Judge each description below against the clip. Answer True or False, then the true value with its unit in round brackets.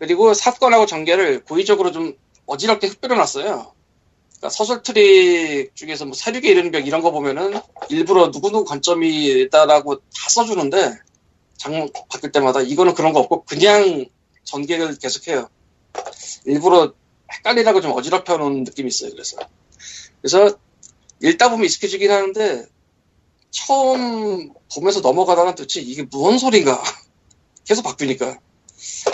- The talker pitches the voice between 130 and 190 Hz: False (200 Hz)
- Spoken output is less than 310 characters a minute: False (325 characters per minute)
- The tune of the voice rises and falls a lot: True (8.4 semitones)